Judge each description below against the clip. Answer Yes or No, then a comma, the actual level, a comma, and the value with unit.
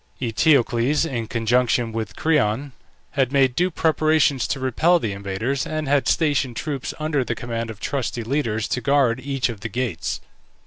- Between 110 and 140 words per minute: No, average, 165 wpm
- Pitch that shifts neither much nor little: Yes, average, 3.9 semitones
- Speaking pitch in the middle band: No, low, 130 Hz